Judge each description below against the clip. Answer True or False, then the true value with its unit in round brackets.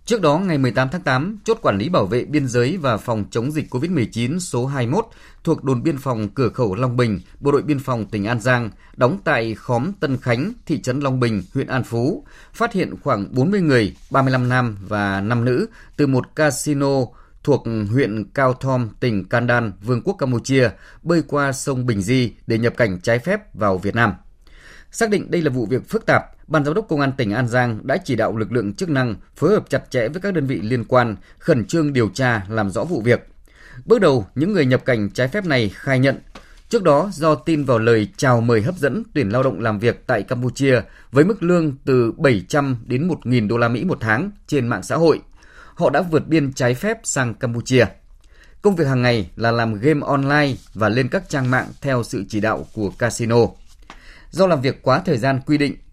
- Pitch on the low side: True (125 Hz)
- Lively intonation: False (4.3 semitones)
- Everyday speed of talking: True (220 wpm)